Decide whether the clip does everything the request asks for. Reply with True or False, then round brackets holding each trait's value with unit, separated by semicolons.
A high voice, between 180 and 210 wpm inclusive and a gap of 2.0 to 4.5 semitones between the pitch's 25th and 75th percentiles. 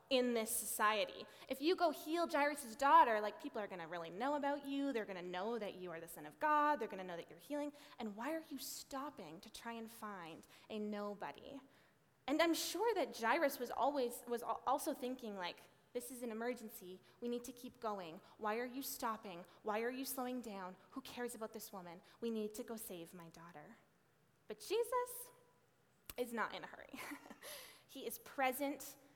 False (235 Hz; 200 wpm; 5.3 semitones)